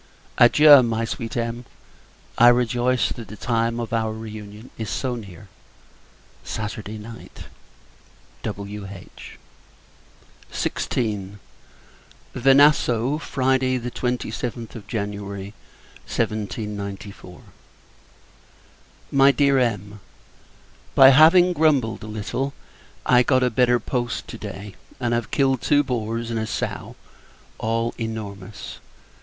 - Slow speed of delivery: Yes, slow, 105 wpm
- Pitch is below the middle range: Yes, low, 115 Hz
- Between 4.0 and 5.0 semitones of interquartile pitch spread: No, average, 3.2 semitones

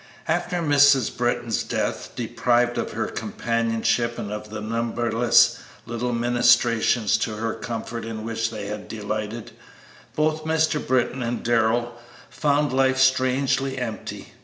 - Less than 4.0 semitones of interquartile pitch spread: Yes, narrow, 2.5 semitones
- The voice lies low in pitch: Yes, low, 120 Hz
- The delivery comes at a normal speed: No, slow, 130 wpm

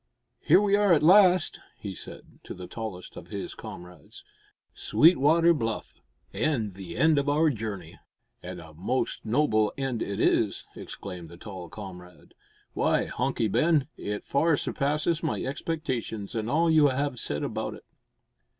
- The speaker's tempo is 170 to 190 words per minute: No, average, 150 wpm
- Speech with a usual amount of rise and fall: No, wide, 7.9 semitones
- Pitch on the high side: No, low, 120 Hz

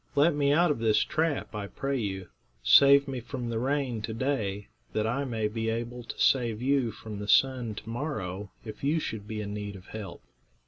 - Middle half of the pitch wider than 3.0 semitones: Yes, average, 4.6 semitones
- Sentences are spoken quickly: Yes, fast, 210 wpm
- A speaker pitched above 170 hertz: No, low, 115 Hz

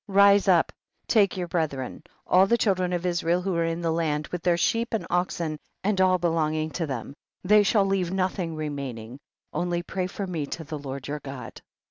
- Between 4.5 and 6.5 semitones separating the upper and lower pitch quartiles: No, average, 3.4 semitones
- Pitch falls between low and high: Yes, medium, 175 Hz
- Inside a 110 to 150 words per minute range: No, fast, 205 wpm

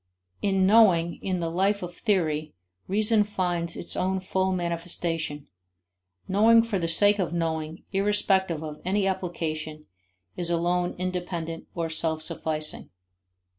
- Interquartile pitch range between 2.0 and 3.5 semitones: Yes, average, 2.7 semitones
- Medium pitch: Yes, medium, 175 Hz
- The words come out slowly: Yes, slow, 130 wpm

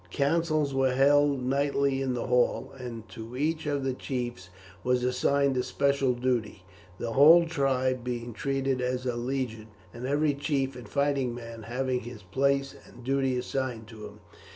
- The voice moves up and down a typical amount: No, narrow, 2.3 semitones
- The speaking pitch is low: Yes, low, 130 Hz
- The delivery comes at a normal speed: Yes, average, 165 wpm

